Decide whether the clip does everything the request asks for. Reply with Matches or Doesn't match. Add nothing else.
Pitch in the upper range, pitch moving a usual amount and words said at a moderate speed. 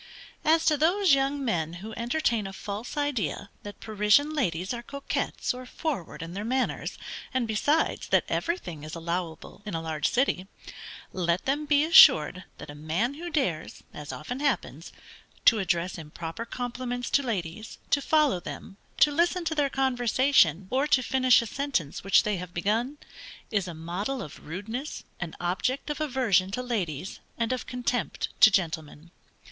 Doesn't match